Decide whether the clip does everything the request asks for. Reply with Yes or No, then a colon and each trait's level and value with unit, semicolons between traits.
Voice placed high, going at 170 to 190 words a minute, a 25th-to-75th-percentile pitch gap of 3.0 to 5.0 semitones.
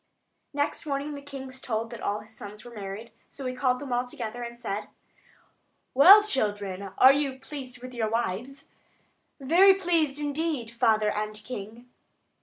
Yes: very high, 250 Hz; average, 175 wpm; average, 4.4 semitones